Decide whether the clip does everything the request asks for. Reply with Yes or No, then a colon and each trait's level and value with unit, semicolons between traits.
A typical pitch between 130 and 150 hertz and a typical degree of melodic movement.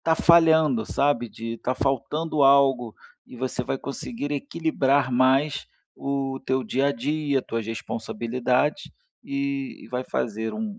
Yes: low, 135 Hz; average, 3.0 semitones